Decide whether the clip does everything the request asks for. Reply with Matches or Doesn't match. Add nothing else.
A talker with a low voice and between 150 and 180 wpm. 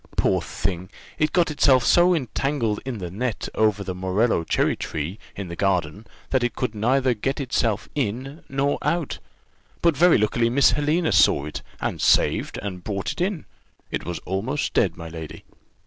Matches